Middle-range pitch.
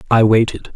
No: low, 110 Hz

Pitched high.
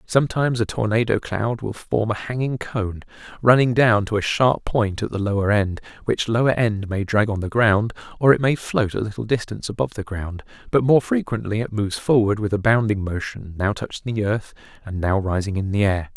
No: low, 110 Hz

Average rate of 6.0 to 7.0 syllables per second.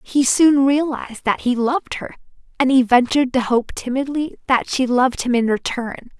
No: 5.1 syllables/s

